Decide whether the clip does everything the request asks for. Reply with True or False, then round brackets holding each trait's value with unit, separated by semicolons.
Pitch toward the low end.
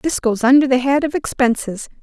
False (260 Hz)